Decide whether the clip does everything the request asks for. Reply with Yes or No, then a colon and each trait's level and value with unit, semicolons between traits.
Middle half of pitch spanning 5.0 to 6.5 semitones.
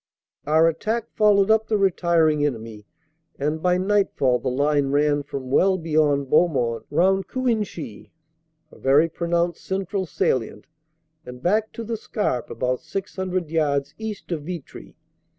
Yes: wide, 5.4 semitones